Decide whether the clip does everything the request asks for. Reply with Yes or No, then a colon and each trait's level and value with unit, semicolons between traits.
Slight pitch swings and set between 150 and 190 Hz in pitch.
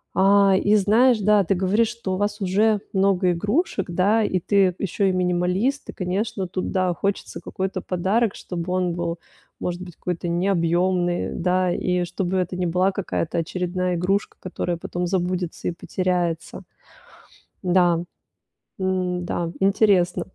Yes: narrow, 2.0 semitones; medium, 185 Hz